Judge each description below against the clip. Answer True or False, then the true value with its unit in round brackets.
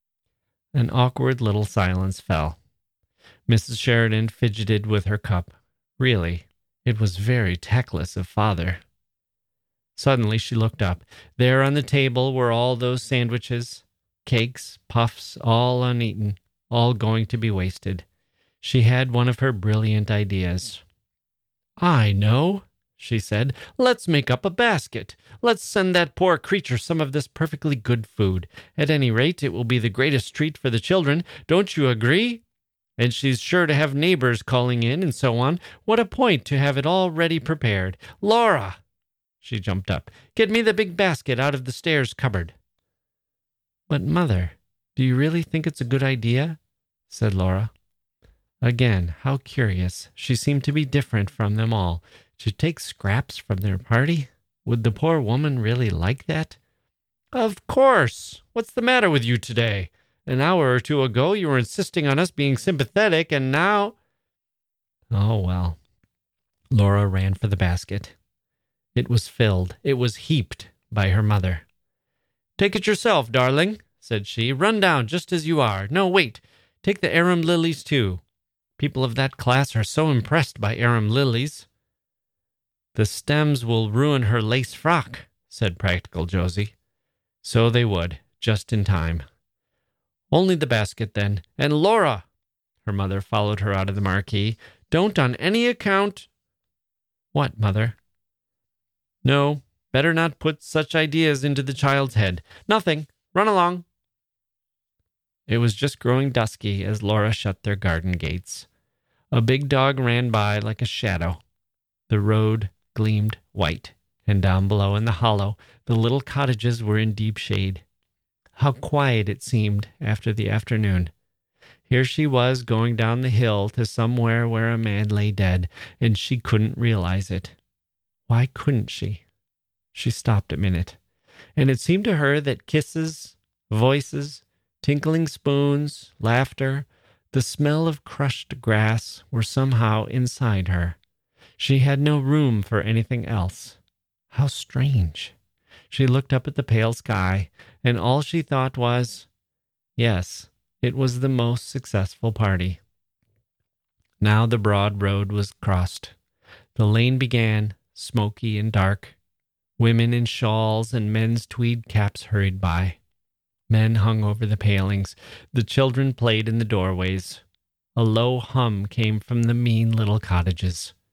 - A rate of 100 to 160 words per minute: True (150 wpm)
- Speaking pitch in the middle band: False (115 Hz)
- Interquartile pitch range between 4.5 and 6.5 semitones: True (5.2 semitones)